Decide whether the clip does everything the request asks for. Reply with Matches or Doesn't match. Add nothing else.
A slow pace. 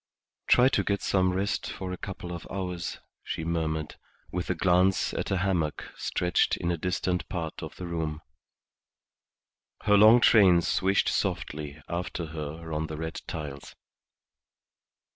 Doesn't match